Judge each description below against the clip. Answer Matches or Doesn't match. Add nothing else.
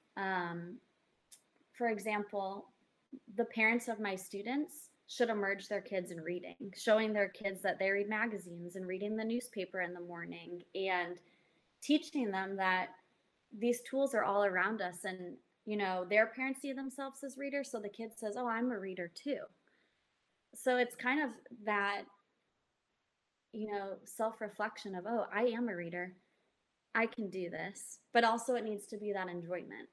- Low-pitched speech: Doesn't match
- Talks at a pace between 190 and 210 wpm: Doesn't match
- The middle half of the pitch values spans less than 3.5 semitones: Doesn't match